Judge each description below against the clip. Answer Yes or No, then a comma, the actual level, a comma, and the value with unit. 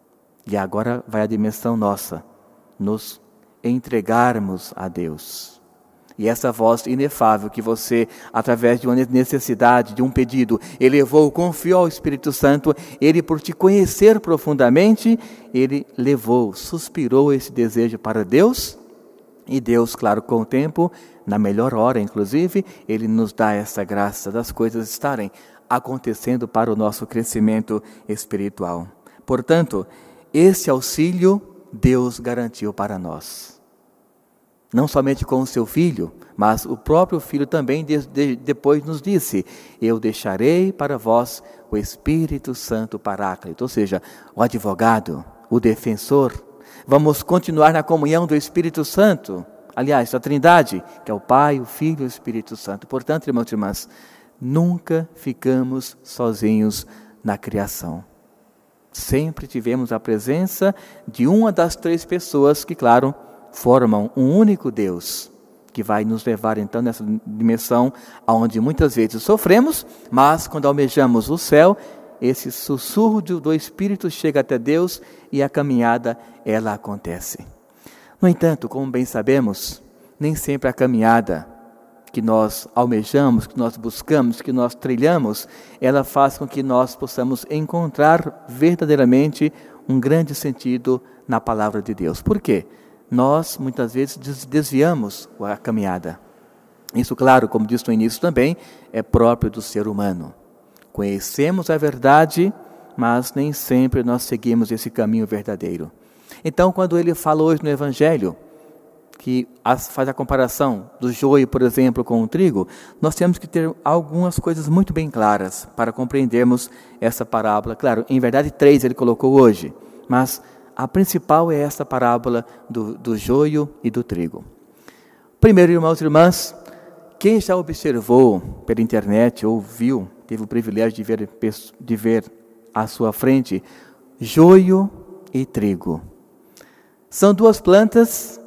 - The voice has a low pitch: Yes, low, 130 Hz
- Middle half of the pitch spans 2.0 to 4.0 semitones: No, average, 5.2 semitones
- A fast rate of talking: No, average, 135 wpm